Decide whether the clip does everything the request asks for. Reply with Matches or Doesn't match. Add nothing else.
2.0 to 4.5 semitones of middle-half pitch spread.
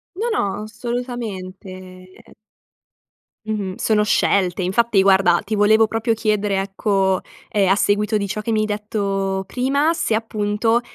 Matches